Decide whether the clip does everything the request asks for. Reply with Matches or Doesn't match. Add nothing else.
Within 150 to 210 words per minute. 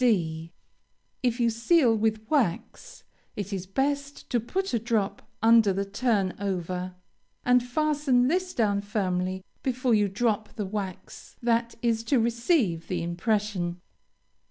Doesn't match